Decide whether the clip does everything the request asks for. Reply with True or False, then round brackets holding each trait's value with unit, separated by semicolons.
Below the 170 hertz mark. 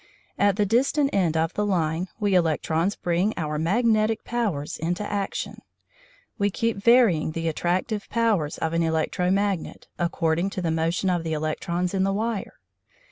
False (185 Hz)